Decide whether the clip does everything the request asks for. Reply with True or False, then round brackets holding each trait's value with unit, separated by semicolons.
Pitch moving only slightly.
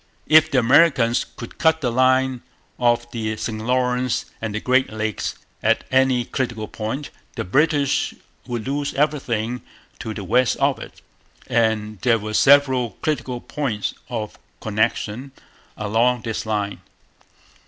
False (3.3 semitones)